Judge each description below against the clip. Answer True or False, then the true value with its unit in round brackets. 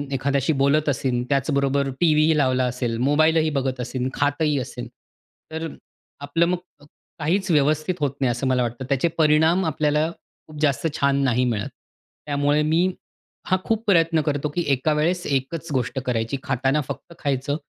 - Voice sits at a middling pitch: True (145 Hz)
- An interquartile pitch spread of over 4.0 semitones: False (3.1 semitones)